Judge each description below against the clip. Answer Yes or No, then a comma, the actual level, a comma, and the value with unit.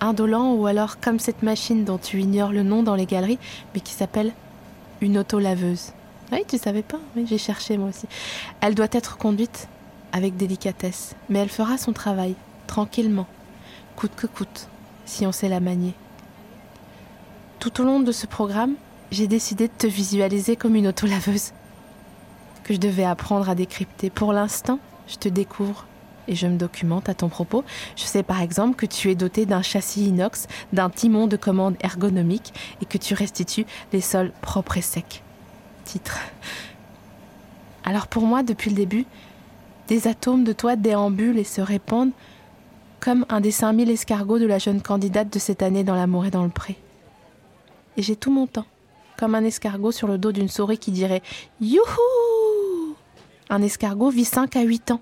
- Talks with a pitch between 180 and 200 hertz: No, high, 210 Hz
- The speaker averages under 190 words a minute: Yes, average, 180 wpm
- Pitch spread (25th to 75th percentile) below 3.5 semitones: Yes, narrow, 2.6 semitones